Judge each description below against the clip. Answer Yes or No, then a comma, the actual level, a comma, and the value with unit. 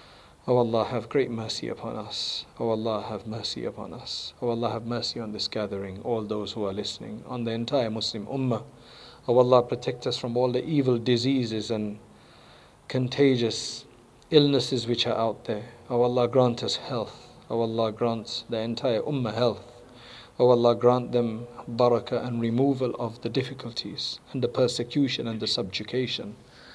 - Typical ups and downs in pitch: No, narrow, 1.8 semitones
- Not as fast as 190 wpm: Yes, average, 180 wpm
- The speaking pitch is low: Yes, low, 120 Hz